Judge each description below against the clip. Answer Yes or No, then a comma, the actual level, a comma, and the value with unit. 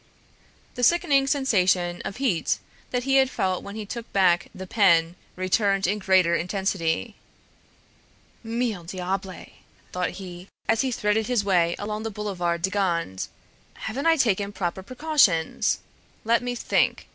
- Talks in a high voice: Yes, high, 200 Hz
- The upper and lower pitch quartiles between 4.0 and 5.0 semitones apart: Yes, average, 4.5 semitones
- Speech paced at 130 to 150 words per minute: Yes, average, 145 wpm